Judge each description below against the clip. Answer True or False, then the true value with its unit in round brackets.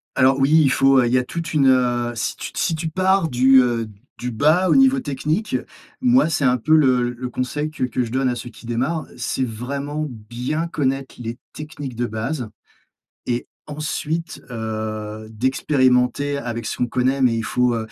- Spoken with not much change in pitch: False (3.8 semitones)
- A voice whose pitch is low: True (130 Hz)